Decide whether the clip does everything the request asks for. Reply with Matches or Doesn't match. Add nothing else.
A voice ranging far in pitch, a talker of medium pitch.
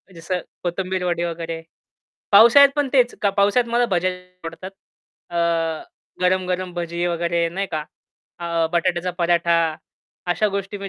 Doesn't match